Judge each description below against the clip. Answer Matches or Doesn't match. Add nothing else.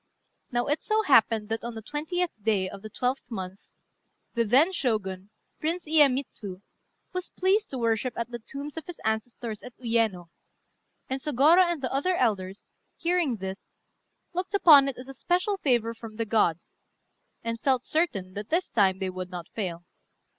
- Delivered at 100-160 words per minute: Doesn't match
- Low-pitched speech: Doesn't match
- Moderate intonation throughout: Doesn't match